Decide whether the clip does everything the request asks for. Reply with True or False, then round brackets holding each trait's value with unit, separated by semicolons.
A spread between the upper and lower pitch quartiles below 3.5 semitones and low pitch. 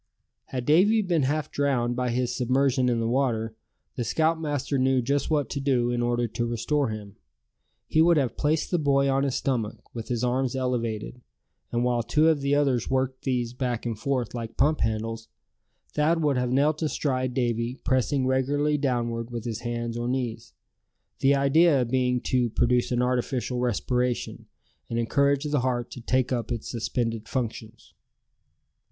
True (2.8 semitones; 125 Hz)